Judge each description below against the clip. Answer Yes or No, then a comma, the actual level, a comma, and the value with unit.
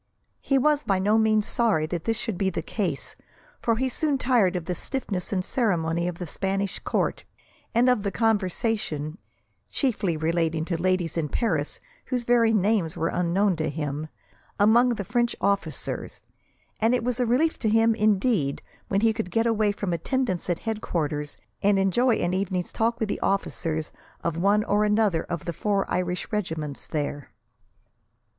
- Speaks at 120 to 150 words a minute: No, average, 170 wpm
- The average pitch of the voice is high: Yes, high, 200 Hz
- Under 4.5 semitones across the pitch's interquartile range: No, average, 4.9 semitones